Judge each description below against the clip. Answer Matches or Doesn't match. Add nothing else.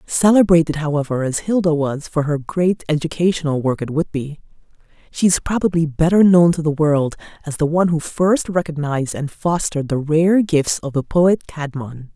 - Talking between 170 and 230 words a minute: Matches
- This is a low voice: Doesn't match